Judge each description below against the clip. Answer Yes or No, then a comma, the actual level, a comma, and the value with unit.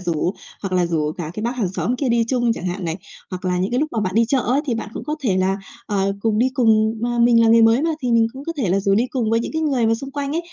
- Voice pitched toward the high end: Yes, high, 225 Hz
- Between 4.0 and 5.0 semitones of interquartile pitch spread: Yes, average, 4.5 semitones